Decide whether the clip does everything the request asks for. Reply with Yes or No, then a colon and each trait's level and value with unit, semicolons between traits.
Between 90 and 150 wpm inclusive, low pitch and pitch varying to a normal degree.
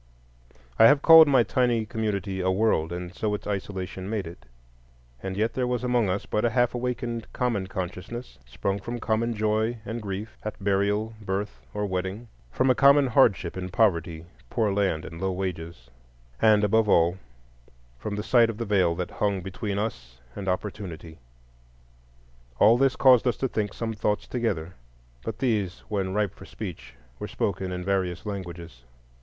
No: average, 170 wpm; low, 105 Hz; average, 3.5 semitones